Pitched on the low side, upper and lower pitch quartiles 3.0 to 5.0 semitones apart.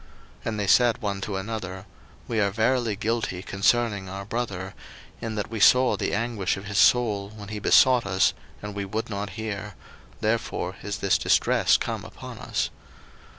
No: low, 105 Hz; narrow, 2.5 semitones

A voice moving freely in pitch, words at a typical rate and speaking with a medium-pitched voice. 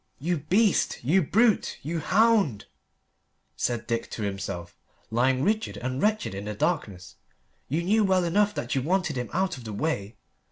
Yes: wide, 8.6 semitones; average, 165 wpm; medium, 150 Hz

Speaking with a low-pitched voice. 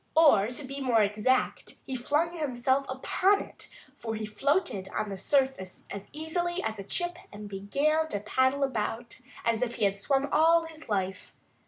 No: very high, 260 Hz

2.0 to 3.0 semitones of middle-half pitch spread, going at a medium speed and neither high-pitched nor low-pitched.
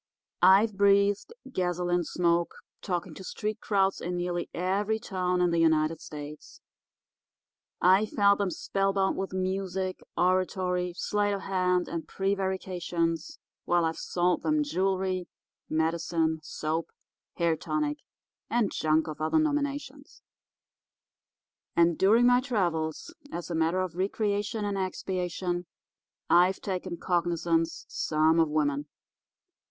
No: average, 2.7 semitones; slow, 120 wpm; medium, 180 Hz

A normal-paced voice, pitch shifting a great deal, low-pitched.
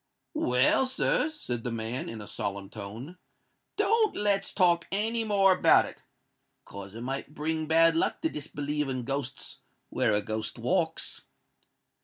No: average, 145 wpm; wide, 8.7 semitones; medium, 150 Hz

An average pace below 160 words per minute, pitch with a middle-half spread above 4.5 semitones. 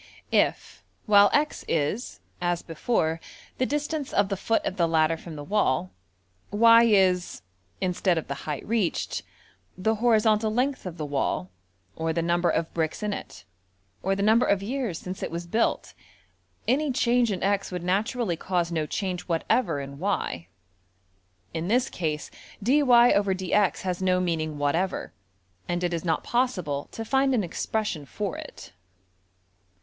Yes: average, 150 wpm; average, 5.2 semitones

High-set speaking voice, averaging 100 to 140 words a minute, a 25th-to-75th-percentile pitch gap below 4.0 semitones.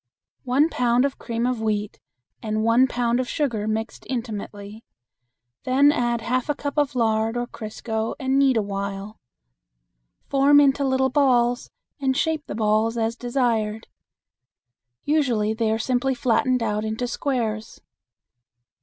Yes: high, 240 Hz; slow, 135 wpm; average, 3.2 semitones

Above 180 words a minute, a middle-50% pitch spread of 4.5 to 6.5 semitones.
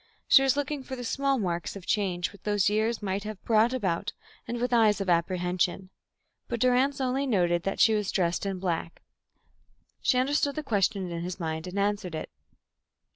Yes: average, 190 wpm; wide, 5.4 semitones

